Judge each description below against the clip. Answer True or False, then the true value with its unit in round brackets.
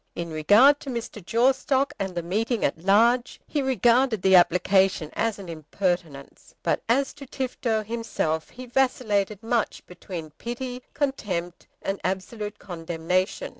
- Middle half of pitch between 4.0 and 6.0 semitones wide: True (5.5 semitones)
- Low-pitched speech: False (210 Hz)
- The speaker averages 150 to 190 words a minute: False (135 wpm)